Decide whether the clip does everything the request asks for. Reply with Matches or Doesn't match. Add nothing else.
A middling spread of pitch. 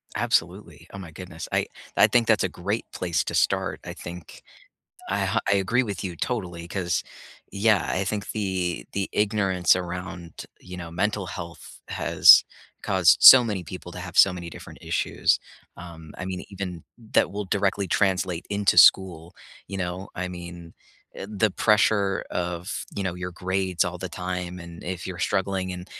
Doesn't match